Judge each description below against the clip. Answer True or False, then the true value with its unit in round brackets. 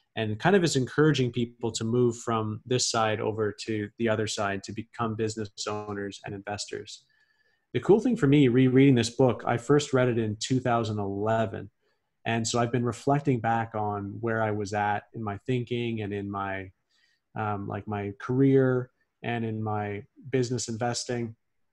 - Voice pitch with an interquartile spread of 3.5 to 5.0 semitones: False (3.1 semitones)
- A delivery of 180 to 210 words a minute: False (170 wpm)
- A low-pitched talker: True (115 Hz)